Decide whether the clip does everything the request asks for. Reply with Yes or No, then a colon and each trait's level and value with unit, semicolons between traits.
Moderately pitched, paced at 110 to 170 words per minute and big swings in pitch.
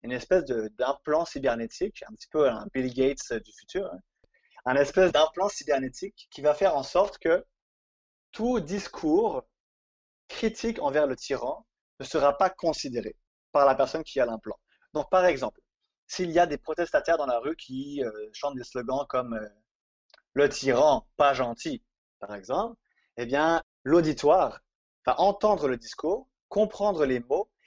Yes: medium, 155 Hz; average, 160 wpm; wide, 7.1 semitones